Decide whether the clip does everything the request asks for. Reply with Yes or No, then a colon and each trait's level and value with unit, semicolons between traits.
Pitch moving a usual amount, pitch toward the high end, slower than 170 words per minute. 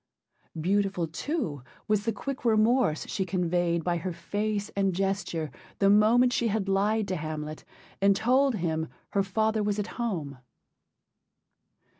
Yes: average, 4.1 semitones; high, 195 Hz; average, 140 wpm